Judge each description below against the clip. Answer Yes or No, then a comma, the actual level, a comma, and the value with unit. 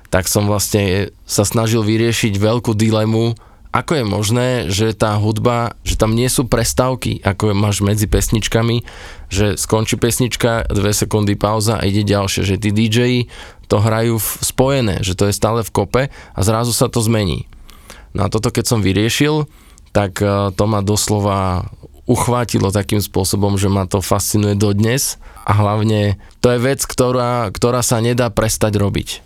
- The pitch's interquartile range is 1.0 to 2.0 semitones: No, narrow, 2.6 semitones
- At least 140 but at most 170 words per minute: Yes, fast, 165 wpm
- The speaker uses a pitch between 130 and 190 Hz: No, low, 110 Hz